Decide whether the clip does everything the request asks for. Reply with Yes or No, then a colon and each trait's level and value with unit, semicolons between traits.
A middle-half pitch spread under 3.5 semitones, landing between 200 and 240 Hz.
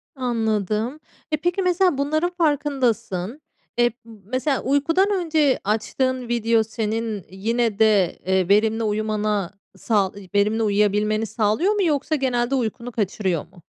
No: average, 4.7 semitones; high, 230 Hz